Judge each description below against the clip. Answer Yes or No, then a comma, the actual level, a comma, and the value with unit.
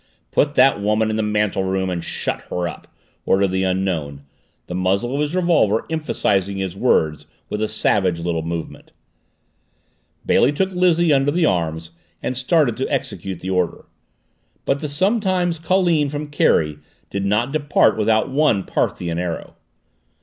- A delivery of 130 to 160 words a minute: Yes, average, 155 wpm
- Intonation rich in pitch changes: Yes, wide, 8.2 semitones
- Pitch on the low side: Yes, low, 105 Hz